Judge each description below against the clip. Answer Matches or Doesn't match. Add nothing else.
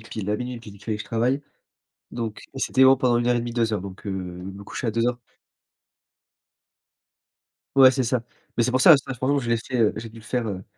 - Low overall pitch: Matches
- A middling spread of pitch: Matches